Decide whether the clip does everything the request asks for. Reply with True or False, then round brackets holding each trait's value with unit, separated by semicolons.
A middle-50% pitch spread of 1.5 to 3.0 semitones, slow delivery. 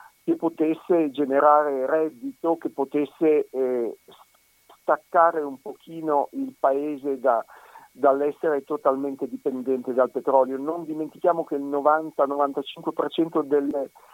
True (2.4 semitones; 100 wpm)